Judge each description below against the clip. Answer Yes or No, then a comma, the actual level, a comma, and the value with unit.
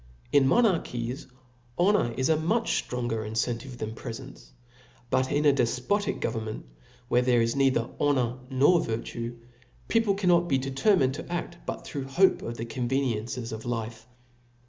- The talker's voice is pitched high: No, low, 130 Hz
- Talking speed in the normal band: Yes, average, 145 wpm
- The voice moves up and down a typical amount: Yes, average, 4.0 semitones